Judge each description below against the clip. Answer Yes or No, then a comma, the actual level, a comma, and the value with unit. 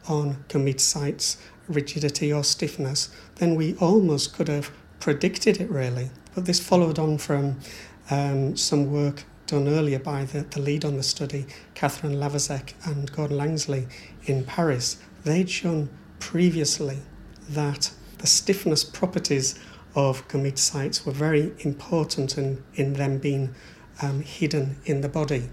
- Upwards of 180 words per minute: No, average, 140 wpm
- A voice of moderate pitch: Yes, medium, 145 Hz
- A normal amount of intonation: No, narrow, 2.1 semitones